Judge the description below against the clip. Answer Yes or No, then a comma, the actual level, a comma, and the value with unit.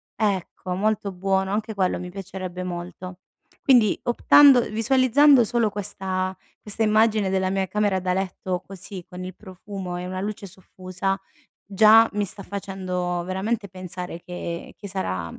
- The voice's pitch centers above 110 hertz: Yes, high, 190 Hz